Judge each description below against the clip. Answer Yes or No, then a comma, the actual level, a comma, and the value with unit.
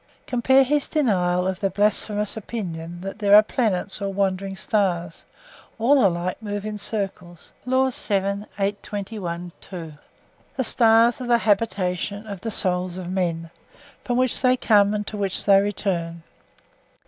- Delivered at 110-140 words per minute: Yes, slow, 135 wpm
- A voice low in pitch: No, high, 200 Hz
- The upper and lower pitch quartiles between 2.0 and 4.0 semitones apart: Yes, average, 3.3 semitones